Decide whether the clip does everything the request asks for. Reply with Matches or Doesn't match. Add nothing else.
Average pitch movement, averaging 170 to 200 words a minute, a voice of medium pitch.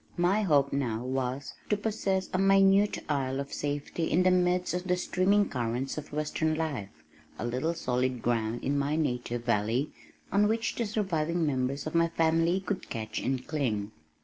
Doesn't match